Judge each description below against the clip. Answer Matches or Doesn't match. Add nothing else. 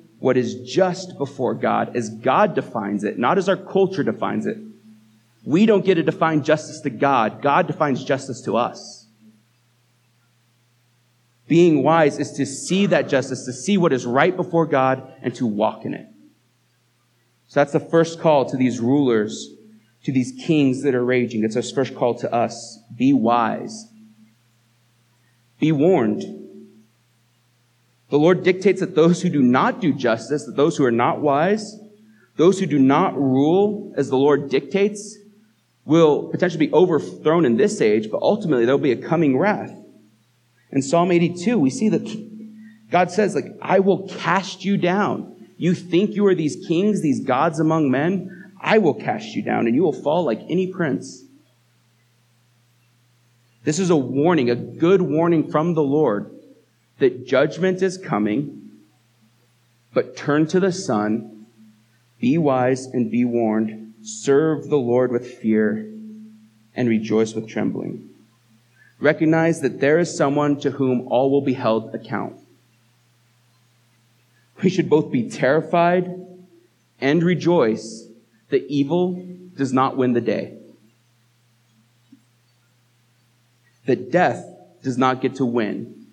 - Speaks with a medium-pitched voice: Doesn't match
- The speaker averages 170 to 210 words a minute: Doesn't match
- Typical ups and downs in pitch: Doesn't match